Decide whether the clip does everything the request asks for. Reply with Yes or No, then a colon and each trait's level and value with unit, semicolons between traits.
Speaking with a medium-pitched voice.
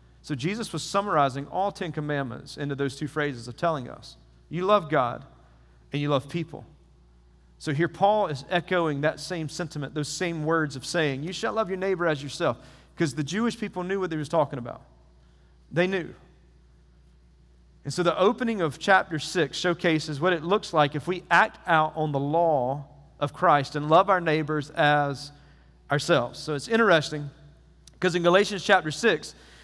Yes: medium, 155 Hz